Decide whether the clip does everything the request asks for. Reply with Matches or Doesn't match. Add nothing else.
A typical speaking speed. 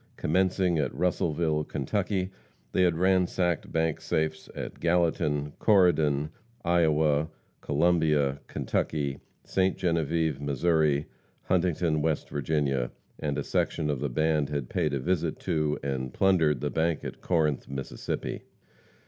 Doesn't match